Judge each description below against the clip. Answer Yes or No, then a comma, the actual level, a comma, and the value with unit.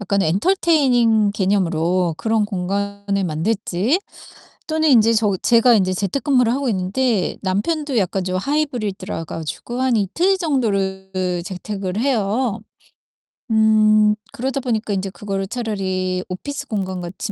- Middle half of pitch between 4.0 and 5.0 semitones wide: Yes, average, 4.4 semitones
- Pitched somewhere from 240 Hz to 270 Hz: No, high, 205 Hz